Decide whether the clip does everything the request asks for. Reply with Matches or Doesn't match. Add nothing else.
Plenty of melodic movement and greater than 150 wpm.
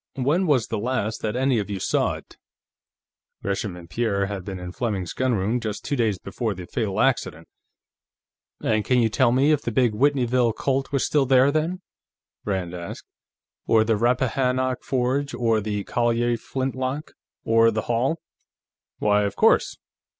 Doesn't match